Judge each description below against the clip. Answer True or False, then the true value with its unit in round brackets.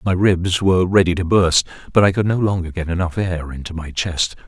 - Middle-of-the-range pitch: False (90 Hz)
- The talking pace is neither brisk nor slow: False (230 wpm)